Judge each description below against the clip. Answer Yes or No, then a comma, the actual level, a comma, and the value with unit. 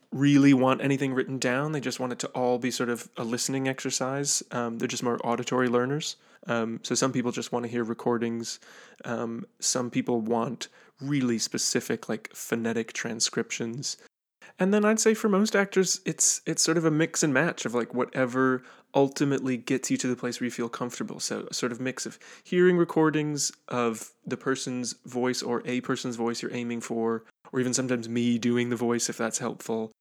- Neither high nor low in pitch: No, low, 125 Hz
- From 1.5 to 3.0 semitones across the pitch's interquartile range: Yes, narrow, 2.5 semitones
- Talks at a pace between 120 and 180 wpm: No, average, 195 wpm